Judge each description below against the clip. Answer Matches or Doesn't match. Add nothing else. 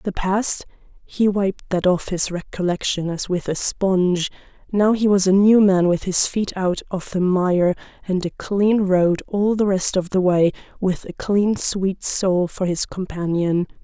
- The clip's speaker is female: Matches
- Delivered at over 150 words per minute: Matches